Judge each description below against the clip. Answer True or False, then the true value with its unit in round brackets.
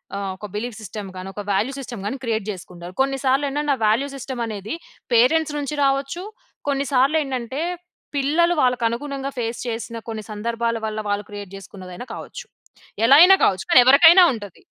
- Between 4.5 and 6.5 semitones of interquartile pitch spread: True (4.9 semitones)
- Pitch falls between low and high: False (240 Hz)